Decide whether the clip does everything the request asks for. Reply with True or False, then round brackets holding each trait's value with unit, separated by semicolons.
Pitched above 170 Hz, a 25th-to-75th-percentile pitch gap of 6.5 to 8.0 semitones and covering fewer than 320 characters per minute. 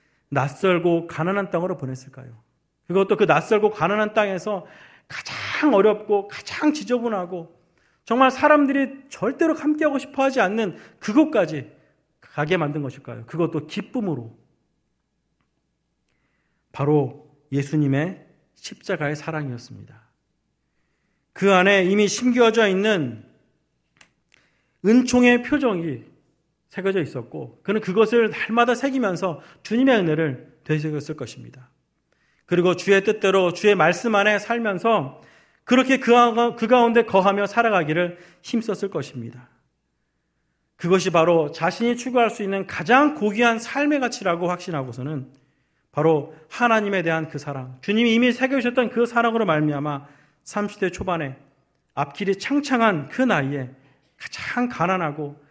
True (185 Hz; 7.4 semitones; 285 characters per minute)